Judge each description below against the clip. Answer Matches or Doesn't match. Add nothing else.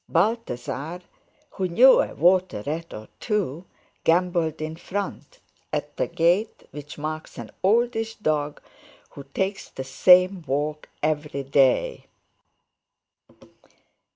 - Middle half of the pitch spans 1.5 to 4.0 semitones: Doesn't match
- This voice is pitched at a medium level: Matches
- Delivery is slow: Matches